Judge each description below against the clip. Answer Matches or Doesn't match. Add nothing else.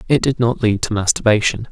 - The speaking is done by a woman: Doesn't match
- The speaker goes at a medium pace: Doesn't match